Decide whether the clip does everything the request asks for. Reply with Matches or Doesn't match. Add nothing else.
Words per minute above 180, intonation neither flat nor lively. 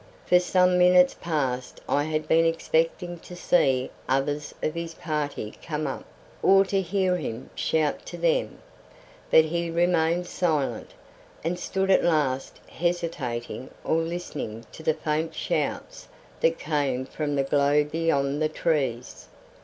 Doesn't match